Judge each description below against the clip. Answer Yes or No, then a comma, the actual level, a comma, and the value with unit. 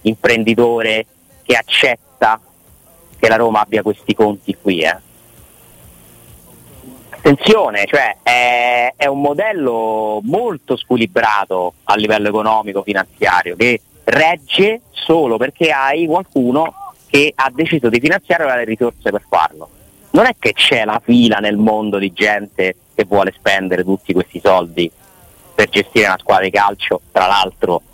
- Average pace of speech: Yes, average, 135 wpm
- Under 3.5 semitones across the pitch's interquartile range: No, average, 3.8 semitones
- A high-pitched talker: No, low, 110 Hz